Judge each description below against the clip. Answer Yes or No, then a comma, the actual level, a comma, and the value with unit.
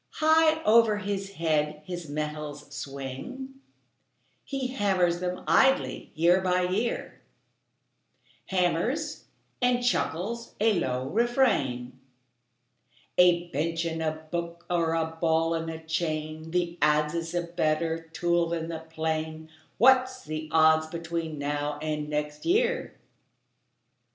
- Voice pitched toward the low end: No, medium, 165 Hz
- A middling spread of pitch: Yes, average, 4.0 semitones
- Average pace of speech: No, slow, 120 wpm